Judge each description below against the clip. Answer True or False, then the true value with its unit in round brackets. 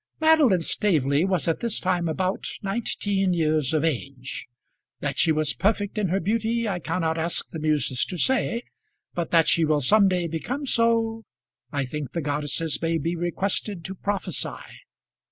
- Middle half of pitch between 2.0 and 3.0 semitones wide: False (4.6 semitones)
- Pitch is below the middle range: False (175 Hz)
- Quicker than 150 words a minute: True (165 wpm)